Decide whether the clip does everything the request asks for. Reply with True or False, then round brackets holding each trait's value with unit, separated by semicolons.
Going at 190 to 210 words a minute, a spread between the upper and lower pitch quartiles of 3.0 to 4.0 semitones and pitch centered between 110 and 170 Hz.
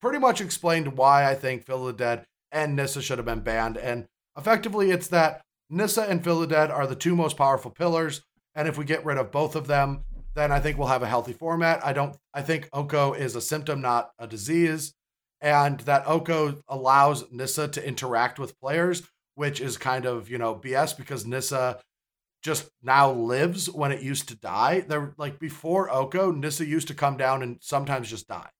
True (205 wpm; 3.4 semitones; 140 Hz)